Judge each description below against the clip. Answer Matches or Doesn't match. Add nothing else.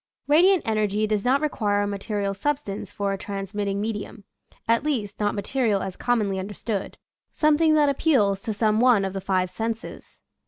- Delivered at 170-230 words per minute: Matches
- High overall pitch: Matches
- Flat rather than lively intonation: Doesn't match